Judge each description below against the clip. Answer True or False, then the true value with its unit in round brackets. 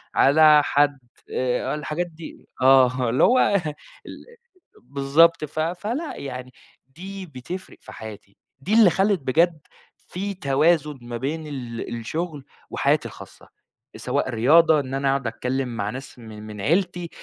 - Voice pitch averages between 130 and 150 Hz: True (140 Hz)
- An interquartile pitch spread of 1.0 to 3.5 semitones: False (4.8 semitones)